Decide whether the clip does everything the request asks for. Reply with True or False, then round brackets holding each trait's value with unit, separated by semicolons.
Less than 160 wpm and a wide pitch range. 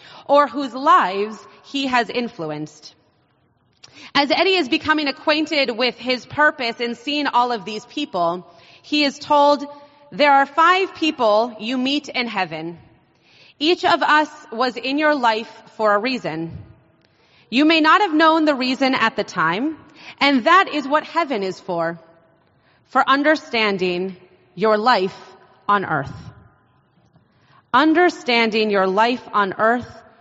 True (135 wpm; 7.9 semitones)